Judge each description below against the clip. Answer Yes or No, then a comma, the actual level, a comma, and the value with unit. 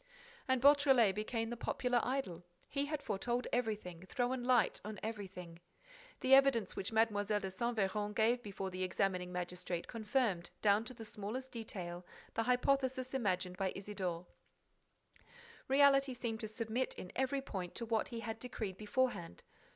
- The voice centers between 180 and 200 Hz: No, high, 220 Hz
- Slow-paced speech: No, average, 150 wpm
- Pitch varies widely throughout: No, average, 4.6 semitones